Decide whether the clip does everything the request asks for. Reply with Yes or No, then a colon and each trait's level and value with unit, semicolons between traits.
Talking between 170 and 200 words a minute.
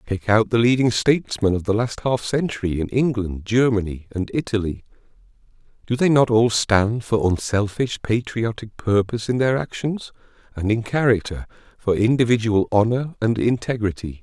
No: average, 150 wpm